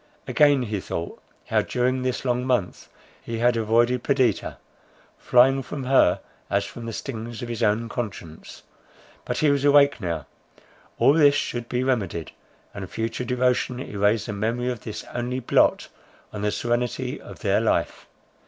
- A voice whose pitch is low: Yes, low, 120 Hz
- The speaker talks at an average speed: Yes, average, 160 wpm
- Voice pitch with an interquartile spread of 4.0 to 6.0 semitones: No, average, 2.8 semitones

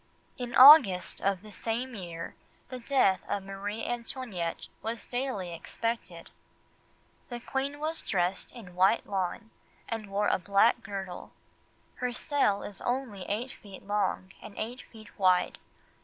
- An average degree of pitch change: Yes, average, 4.2 semitones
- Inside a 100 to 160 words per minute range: Yes, average, 140 wpm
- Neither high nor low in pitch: No, high, 210 Hz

